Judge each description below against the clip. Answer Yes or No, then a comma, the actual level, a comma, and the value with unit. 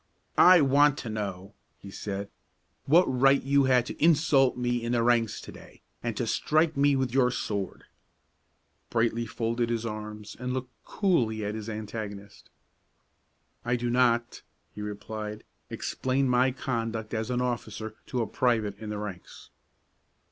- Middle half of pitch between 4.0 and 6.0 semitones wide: No, average, 3.3 semitones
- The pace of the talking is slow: No, average, 155 wpm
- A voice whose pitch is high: No, low, 120 Hz